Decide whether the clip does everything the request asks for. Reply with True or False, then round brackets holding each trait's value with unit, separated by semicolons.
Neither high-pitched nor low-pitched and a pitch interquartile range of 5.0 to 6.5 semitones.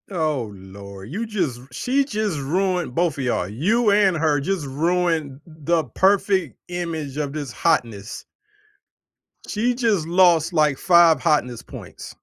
True (165 Hz; 5.3 semitones)